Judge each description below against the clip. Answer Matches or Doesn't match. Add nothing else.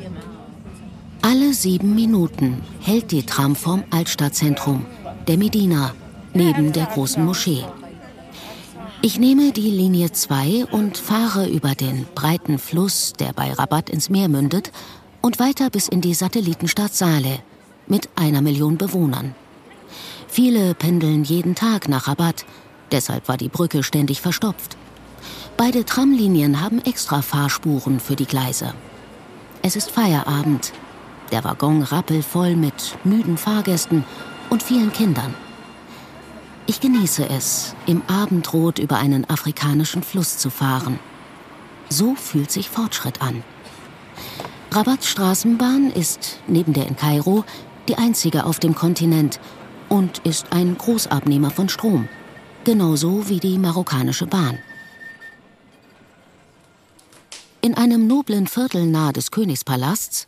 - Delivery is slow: Matches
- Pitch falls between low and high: Matches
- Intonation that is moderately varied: Doesn't match